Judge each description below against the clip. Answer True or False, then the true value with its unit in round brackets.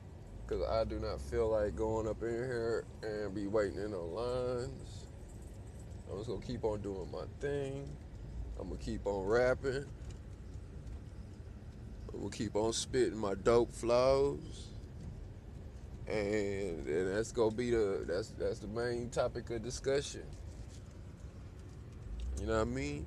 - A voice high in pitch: False (110 Hz)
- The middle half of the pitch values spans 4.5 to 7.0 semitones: False (3.4 semitones)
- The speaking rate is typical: True (145 wpm)